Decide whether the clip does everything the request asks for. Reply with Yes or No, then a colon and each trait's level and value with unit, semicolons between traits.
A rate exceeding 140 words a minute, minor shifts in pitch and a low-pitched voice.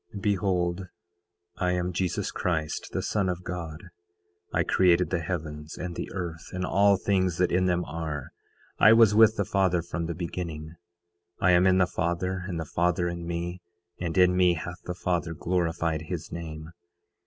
Yes: average, 175 wpm; narrow, 1.6 semitones; very low, 90 Hz